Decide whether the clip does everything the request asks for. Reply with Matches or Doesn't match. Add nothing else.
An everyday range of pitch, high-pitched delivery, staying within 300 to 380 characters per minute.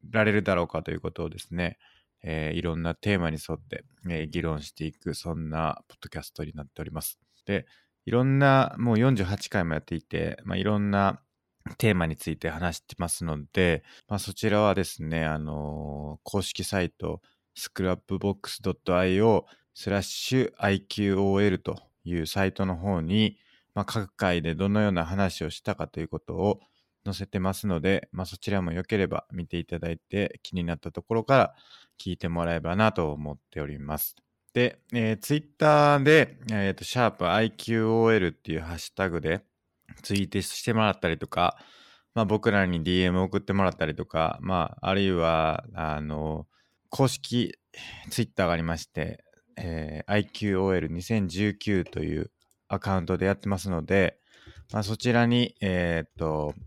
Doesn't match